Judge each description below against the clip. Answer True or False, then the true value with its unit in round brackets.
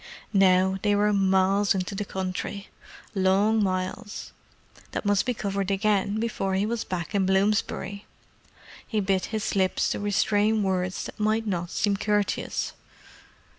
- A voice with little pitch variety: True (1.7 semitones)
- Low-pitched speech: False (200 Hz)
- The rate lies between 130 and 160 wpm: True (135 wpm)